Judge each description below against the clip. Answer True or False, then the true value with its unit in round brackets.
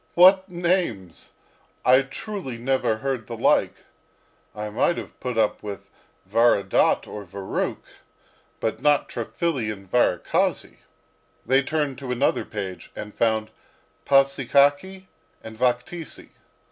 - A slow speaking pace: True (115 wpm)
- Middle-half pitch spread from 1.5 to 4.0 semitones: False (4.7 semitones)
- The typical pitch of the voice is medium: False (125 Hz)